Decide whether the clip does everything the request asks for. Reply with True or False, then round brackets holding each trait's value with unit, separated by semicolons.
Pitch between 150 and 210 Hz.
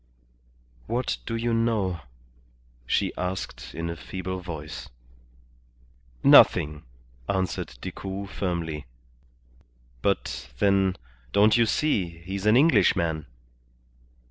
False (95 Hz)